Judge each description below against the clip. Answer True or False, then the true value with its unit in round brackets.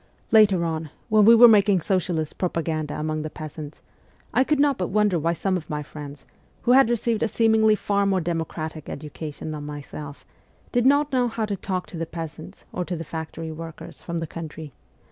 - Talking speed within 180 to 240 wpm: True (195 wpm)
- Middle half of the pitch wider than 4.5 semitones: True (5.3 semitones)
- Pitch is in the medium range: True (170 Hz)